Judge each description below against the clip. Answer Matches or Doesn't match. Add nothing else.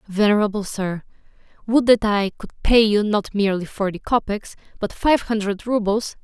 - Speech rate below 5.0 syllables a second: Doesn't match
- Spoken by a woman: Matches